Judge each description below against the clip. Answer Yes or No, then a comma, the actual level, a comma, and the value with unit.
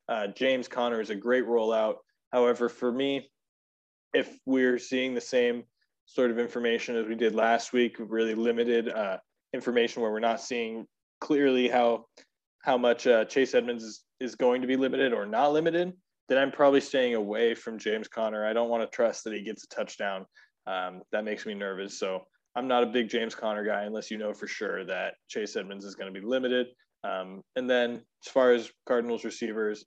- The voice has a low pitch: Yes, low, 120 Hz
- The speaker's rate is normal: Yes, average, 195 wpm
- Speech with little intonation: Yes, narrow, 2.3 semitones